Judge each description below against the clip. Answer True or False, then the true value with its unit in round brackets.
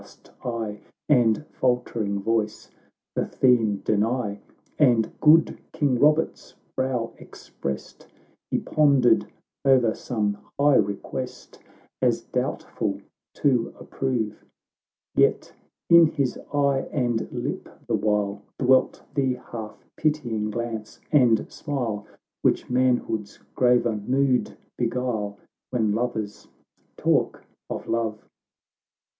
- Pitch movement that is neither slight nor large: True (3.4 semitones)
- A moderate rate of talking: False (100 wpm)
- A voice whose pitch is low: True (120 Hz)